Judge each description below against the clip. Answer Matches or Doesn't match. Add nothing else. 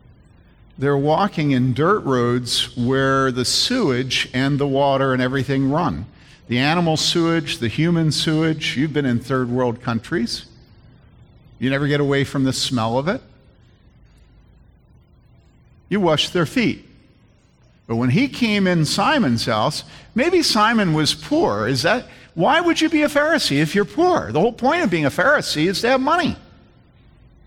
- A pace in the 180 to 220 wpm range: Doesn't match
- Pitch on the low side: Doesn't match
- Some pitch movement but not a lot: Doesn't match